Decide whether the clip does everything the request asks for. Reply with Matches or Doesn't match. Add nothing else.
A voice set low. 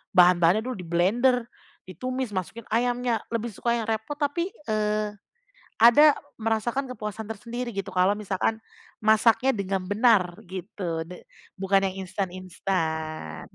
Doesn't match